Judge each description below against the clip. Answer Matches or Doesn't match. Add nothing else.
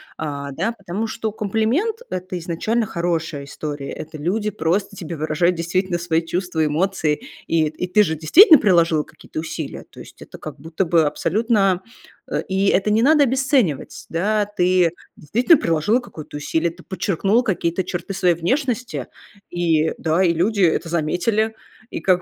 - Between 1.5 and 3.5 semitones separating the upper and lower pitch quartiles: Doesn't match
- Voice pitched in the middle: Matches